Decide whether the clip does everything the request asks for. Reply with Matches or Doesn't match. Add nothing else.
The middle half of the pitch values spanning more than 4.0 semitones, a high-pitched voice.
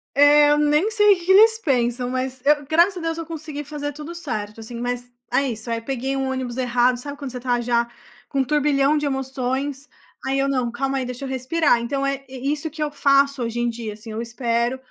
Doesn't match